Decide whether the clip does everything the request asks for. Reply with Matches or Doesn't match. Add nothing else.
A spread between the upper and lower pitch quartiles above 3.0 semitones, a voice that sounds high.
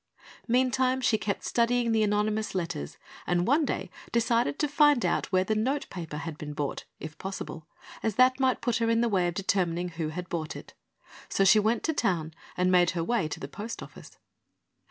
Matches